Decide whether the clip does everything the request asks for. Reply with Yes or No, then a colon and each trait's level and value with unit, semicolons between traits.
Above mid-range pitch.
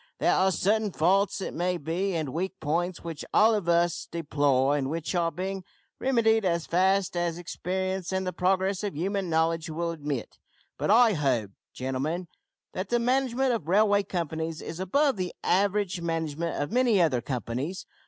No: medium, 180 Hz